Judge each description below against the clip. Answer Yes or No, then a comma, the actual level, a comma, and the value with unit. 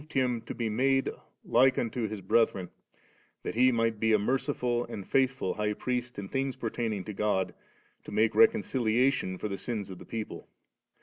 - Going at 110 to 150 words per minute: No, average, 180 wpm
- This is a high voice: No, low, 115 Hz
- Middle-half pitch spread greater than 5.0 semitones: No, average, 3.3 semitones